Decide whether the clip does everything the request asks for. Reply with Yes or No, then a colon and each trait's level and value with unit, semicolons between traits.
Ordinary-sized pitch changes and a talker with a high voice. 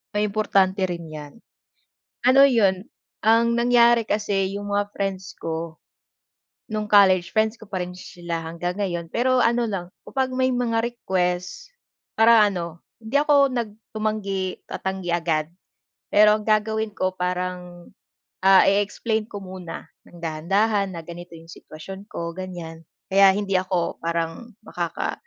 Yes: average, 3.7 semitones; high, 195 Hz